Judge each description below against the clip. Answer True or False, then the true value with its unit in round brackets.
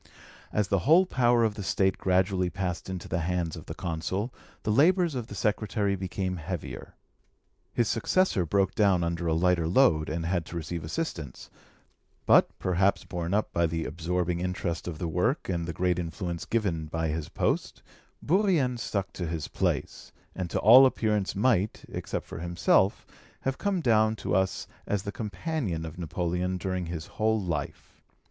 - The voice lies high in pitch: False (95 Hz)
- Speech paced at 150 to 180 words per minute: True (170 wpm)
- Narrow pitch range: False (4.1 semitones)